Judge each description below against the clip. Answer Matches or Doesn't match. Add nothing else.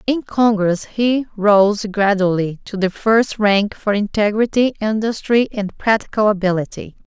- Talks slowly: Matches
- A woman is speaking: Matches